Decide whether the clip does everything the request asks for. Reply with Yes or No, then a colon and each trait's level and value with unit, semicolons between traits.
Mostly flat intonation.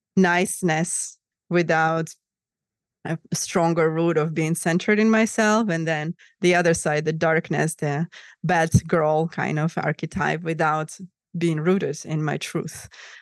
Yes: narrow, 2.2 semitones